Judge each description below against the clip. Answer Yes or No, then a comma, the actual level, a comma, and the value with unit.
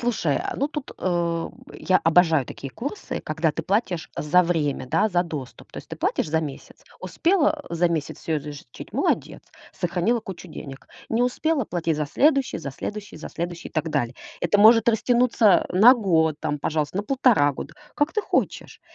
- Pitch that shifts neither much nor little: No, wide, 6.7 semitones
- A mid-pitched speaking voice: Yes, medium, 175 Hz